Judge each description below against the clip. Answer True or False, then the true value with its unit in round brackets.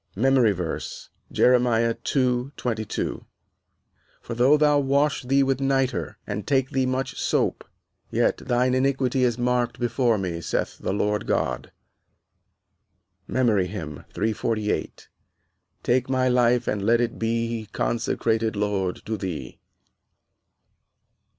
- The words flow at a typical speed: False (115 wpm)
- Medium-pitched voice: False (120 Hz)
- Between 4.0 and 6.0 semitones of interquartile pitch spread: False (3.1 semitones)